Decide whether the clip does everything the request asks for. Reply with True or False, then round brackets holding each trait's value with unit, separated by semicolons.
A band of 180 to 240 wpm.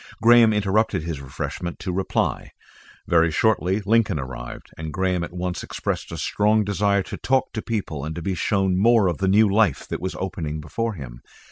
True (190 wpm)